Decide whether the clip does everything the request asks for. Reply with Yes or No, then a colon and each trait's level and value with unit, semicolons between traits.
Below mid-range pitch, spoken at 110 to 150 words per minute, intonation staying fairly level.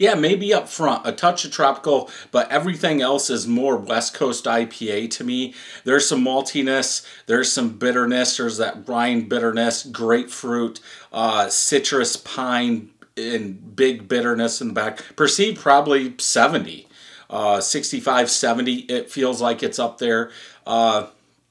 No: low, 125 Hz; average, 140 wpm; average, 3.2 semitones